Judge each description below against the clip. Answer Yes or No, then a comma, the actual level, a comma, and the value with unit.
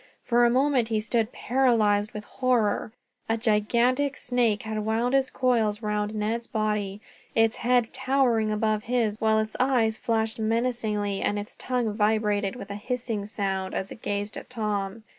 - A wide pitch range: No, narrow, 2.4 semitones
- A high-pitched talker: Yes, high, 220 Hz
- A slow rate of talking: No, average, 160 wpm